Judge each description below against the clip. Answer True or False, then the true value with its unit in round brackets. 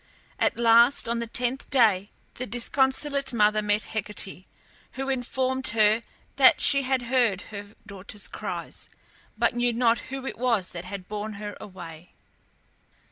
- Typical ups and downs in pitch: True (3.6 semitones)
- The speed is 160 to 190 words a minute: False (145 wpm)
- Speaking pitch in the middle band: False (230 Hz)